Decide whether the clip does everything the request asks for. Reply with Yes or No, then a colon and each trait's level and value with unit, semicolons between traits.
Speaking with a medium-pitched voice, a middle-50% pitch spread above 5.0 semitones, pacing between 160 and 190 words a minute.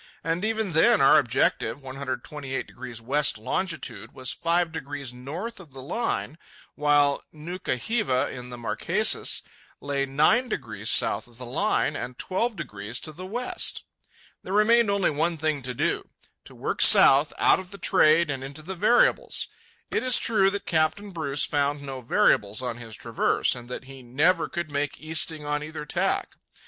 Yes: medium, 150 Hz; wide, 5.4 semitones; average, 165 wpm